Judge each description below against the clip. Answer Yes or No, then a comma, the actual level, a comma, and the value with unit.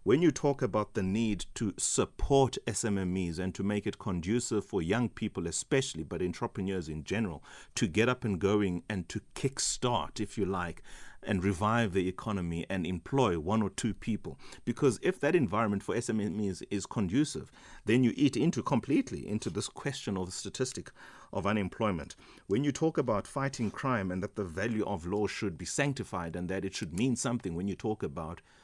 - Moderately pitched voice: No, low, 105 Hz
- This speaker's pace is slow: No, average, 190 wpm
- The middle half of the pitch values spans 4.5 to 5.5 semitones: No, average, 3.9 semitones